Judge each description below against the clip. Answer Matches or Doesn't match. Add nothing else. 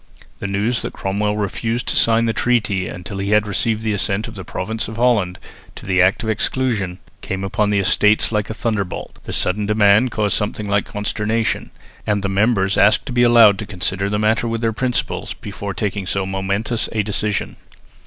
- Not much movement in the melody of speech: Matches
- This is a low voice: Matches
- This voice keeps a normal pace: Matches